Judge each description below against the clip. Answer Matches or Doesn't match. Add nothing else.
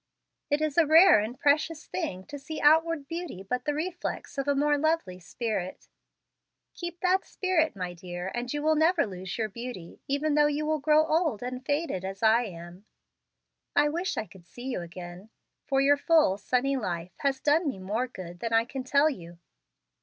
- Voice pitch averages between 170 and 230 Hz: Doesn't match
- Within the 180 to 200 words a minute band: Matches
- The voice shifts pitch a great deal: Matches